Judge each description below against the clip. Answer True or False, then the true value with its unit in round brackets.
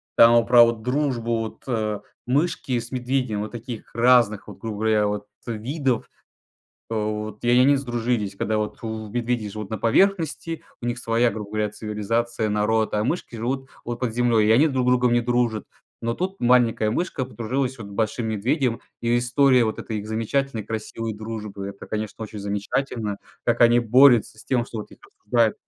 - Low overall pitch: True (115 Hz)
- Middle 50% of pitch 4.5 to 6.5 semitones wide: False (2.5 semitones)